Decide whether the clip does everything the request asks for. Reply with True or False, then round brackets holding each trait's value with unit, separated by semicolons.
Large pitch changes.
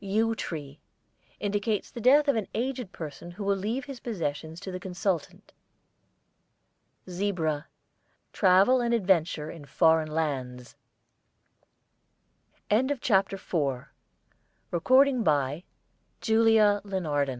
True (6.0 semitones)